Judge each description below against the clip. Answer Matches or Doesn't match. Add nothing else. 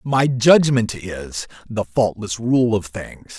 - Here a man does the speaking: Matches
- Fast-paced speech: Doesn't match